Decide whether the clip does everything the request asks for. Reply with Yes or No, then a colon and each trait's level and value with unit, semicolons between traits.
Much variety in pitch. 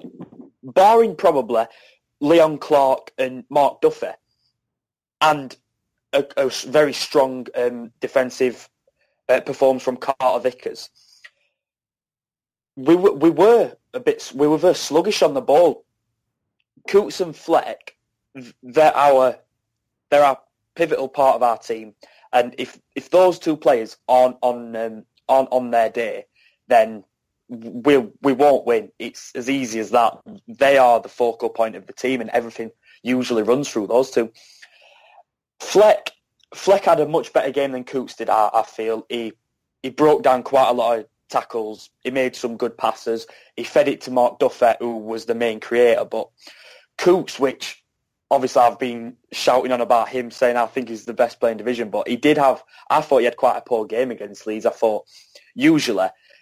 No: average, 3.9 semitones